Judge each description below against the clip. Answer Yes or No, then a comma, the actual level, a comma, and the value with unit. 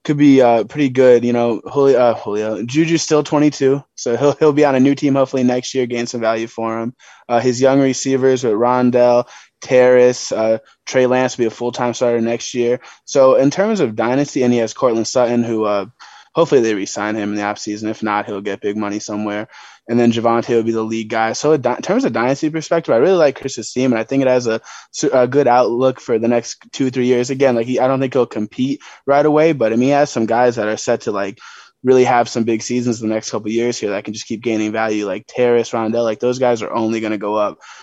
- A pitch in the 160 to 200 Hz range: No, low, 120 Hz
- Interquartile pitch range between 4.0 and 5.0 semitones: No, average, 2.8 semitones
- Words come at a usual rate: No, fast, 250 wpm